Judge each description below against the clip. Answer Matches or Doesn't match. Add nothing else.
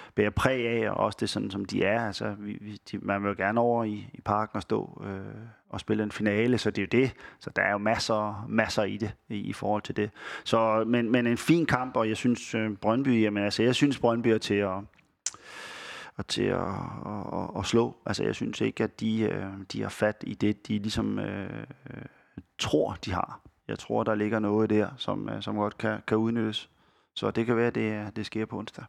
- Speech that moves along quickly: Matches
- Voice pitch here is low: Matches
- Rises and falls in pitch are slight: Matches